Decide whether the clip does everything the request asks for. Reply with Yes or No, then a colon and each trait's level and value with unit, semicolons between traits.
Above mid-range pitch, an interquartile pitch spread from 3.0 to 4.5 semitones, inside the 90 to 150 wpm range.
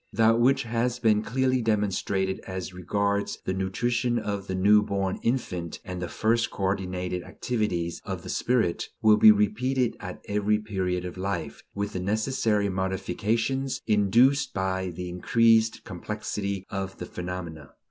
No: low, 100 Hz; average, 3.4 semitones; average, 145 wpm